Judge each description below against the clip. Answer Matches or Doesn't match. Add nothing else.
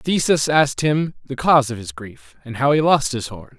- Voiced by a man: Matches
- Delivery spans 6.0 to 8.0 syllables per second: Doesn't match